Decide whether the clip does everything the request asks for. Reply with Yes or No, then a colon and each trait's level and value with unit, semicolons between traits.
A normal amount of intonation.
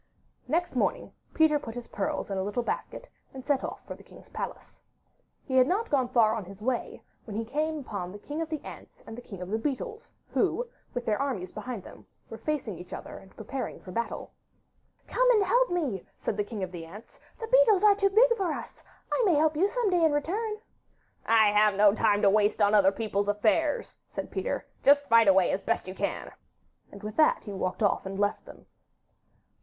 No: wide, 7.6 semitones